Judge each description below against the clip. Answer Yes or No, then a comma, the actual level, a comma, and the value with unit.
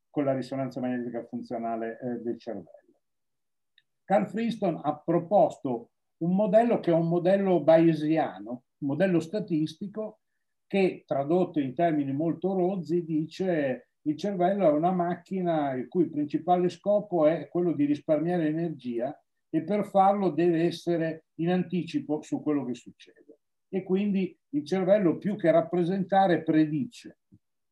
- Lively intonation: No, average, 4.1 semitones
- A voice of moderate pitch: Yes, medium, 170 Hz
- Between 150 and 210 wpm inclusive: No, average, 135 wpm